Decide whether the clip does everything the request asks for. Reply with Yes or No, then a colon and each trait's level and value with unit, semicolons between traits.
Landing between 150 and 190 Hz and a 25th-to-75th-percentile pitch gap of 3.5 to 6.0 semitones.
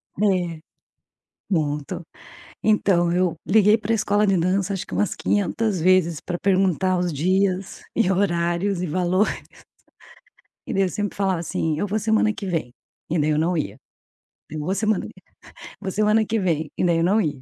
No: medium, 185 Hz; average, 3.1 semitones